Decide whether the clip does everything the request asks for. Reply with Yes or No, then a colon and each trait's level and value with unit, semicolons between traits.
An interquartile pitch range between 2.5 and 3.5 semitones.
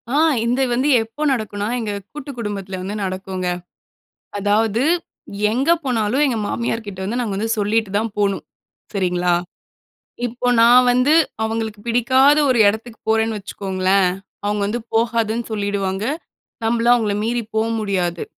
Yes: average, 2.9 semitones